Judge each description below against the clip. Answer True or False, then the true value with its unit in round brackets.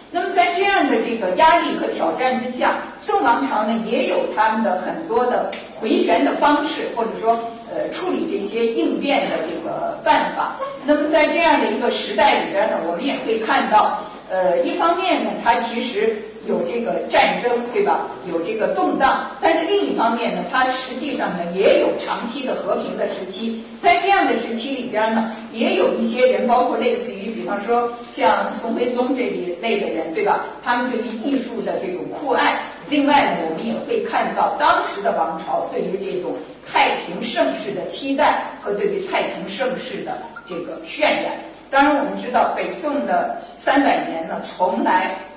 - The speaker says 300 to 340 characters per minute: False (270 characters per minute)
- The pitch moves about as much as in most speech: True (5.0 semitones)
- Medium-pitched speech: False (255 Hz)